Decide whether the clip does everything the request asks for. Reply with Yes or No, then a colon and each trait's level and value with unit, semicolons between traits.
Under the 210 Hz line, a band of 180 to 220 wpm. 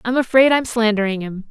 No: high, 230 Hz; average, 200 wpm